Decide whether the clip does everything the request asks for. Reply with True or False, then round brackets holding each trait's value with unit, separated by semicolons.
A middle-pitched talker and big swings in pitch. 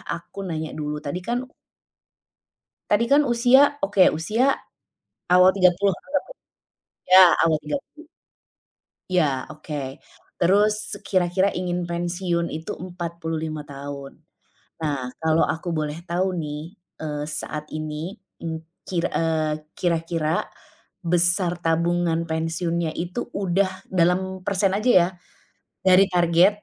False (175 Hz; 2.8 semitones)